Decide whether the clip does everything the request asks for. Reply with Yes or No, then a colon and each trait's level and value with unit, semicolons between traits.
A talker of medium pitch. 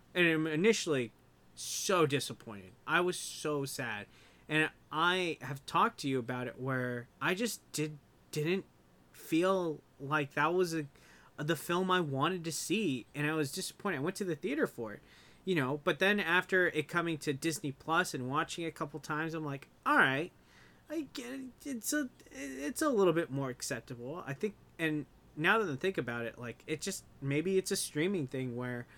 Yes: medium, 155 Hz